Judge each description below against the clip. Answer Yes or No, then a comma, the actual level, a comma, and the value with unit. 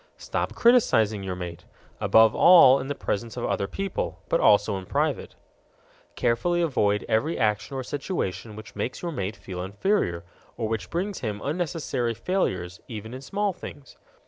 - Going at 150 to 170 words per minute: Yes, average, 160 wpm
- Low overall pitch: Yes, low, 115 Hz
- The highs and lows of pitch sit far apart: Yes, wide, 8.2 semitones